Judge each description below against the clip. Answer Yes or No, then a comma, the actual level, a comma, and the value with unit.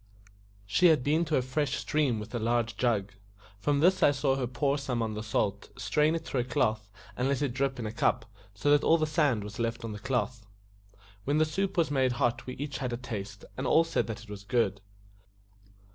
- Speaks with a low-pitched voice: Yes, low, 125 Hz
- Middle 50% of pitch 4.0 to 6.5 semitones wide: Yes, average, 4.5 semitones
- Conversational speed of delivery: No, fast, 230 wpm